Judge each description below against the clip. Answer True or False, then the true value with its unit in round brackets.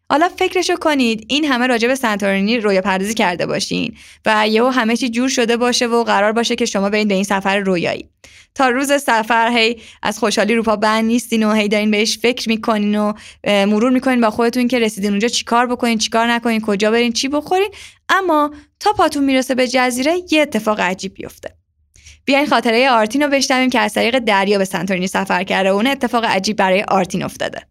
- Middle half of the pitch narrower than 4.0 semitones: True (3.5 semitones)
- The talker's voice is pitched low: False (230 Hz)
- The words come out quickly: True (195 wpm)